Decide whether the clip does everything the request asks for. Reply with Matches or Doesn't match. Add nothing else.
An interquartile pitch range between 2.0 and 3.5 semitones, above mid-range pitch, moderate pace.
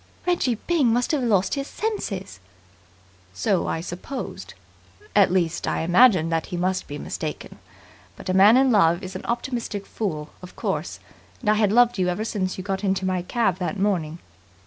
Doesn't match